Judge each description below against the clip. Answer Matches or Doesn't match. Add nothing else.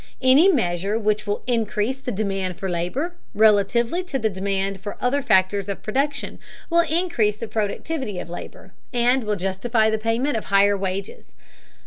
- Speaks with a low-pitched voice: Doesn't match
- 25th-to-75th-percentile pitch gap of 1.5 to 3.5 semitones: Doesn't match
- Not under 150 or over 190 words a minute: Matches